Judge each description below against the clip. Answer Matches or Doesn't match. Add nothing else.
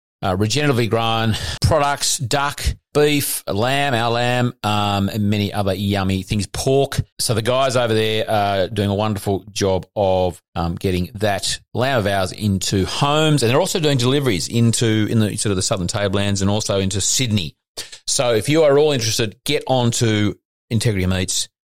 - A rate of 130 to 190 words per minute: Matches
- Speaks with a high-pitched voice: Doesn't match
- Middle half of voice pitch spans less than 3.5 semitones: Doesn't match